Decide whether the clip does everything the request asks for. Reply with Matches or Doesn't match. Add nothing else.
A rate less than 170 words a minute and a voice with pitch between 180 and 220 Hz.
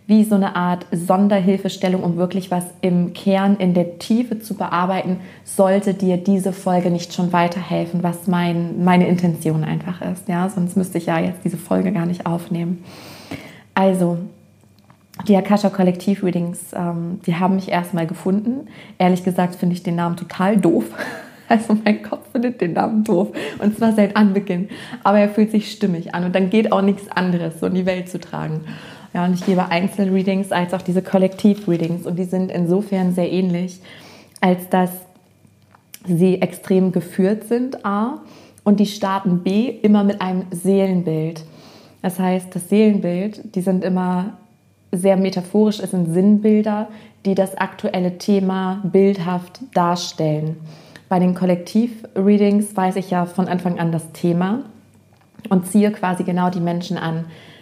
Matches